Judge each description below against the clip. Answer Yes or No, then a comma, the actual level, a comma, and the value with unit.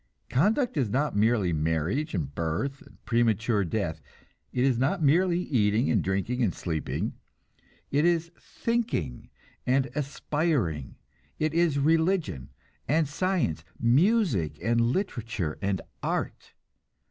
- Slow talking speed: Yes, slow, 120 wpm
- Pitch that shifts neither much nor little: No, wide, 8.6 semitones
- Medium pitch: No, low, 125 Hz